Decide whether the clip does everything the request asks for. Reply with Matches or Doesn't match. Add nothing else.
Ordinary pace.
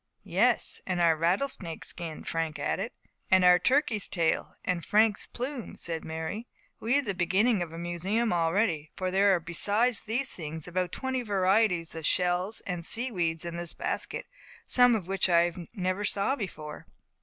Matches